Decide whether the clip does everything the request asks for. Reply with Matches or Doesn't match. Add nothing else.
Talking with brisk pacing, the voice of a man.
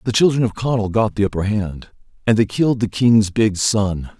Matches